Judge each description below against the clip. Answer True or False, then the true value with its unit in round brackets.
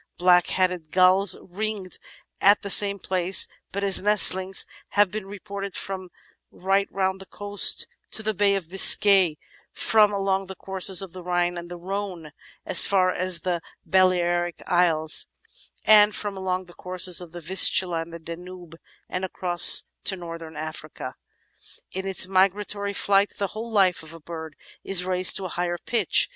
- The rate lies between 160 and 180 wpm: True (170 wpm)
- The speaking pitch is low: False (185 Hz)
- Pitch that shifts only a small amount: True (2.1 semitones)